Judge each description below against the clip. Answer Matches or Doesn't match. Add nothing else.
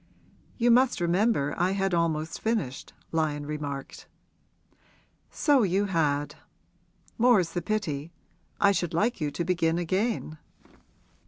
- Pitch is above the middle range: Doesn't match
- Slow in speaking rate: Matches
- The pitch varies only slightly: Doesn't match